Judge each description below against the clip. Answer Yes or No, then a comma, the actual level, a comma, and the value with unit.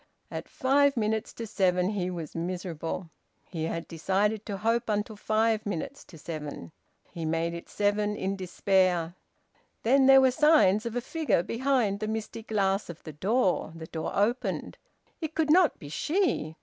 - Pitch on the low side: No, high, 205 Hz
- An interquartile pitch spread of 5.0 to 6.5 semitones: Yes, average, 5.3 semitones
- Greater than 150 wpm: Yes, average, 165 wpm